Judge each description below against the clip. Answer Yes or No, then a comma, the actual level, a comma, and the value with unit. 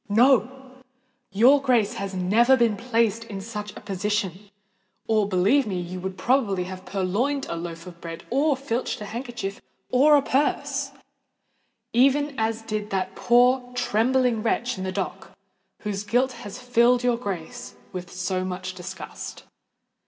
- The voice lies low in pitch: No, high, 225 Hz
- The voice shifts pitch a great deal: No, average, 4.9 semitones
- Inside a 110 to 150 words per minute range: Yes, average, 145 wpm